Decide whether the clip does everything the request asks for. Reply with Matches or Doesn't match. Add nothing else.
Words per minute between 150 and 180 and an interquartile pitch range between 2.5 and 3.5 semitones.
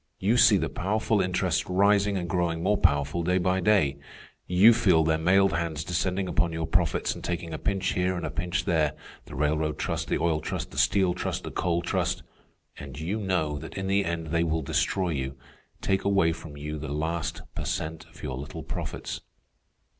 Doesn't match